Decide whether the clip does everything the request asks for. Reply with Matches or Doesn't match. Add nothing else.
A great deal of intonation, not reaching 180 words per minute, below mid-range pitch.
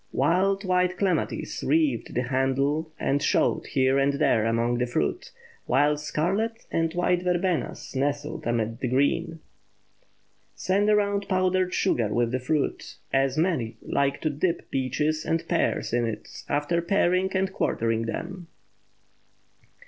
Doesn't match